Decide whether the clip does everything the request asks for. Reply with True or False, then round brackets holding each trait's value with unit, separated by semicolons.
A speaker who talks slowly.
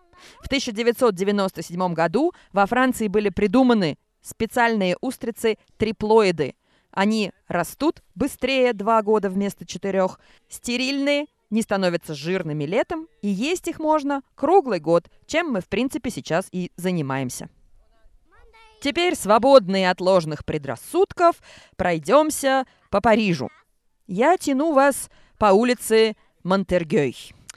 True (105 wpm)